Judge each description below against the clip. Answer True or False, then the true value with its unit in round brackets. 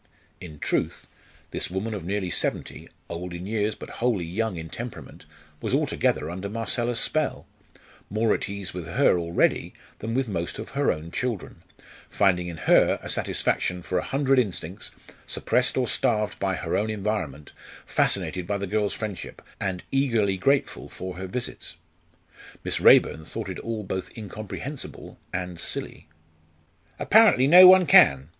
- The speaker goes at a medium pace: True (150 wpm)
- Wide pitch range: False (4.2 semitones)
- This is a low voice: True (100 Hz)